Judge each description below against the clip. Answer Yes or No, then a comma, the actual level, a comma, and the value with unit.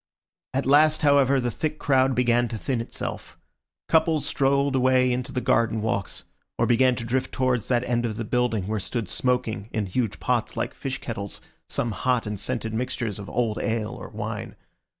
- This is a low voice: Yes, low, 125 Hz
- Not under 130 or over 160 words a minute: No, average, 185 wpm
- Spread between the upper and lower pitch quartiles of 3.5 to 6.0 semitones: No, average, 2.7 semitones